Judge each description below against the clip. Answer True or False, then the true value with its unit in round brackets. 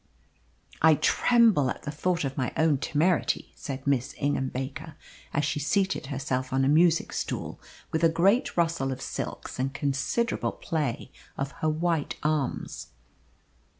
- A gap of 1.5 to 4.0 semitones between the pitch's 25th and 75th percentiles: True (3.5 semitones)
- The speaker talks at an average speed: True (150 wpm)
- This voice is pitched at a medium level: True (150 Hz)